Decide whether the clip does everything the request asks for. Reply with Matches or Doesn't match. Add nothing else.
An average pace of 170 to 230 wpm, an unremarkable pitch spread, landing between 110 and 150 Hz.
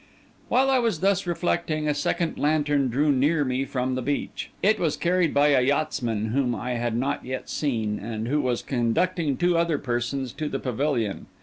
Matches